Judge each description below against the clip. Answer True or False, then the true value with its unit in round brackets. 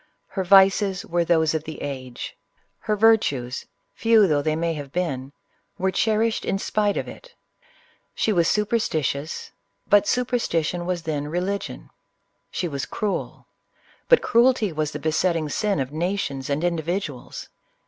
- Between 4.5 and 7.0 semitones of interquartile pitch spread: True (5.1 semitones)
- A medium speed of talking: True (160 wpm)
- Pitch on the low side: False (175 Hz)